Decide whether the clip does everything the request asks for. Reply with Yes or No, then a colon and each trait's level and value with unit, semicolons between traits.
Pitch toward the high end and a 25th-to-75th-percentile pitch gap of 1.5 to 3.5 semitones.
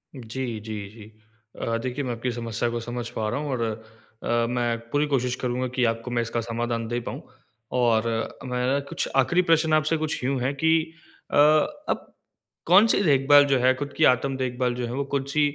No: low, 125 Hz; average, 3.0 semitones